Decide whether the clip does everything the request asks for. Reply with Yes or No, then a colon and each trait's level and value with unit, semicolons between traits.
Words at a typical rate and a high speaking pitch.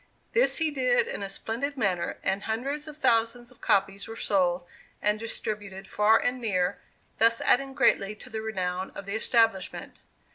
Yes: average, 170 wpm; high, 220 Hz